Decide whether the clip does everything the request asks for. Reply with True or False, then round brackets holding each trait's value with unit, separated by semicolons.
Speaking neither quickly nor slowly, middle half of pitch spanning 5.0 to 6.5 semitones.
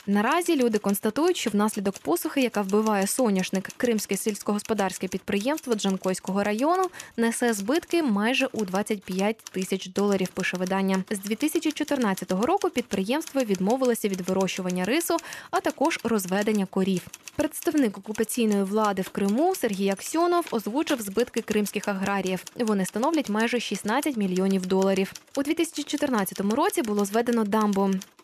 True (125 wpm; 5.5 semitones)